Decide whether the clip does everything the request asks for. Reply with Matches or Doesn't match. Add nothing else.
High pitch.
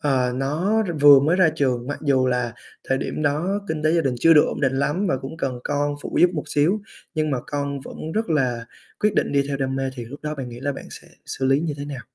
Doesn't match